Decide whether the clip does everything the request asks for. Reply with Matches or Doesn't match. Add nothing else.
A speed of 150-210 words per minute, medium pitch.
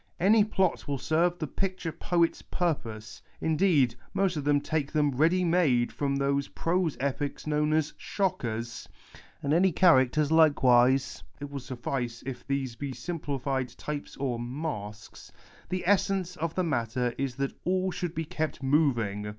Matches